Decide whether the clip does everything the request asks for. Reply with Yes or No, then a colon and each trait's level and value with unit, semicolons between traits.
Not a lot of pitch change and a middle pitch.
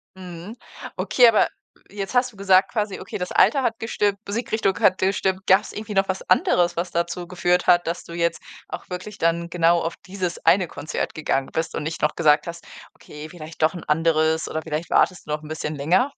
No: average, 3.1 semitones; medium, 175 Hz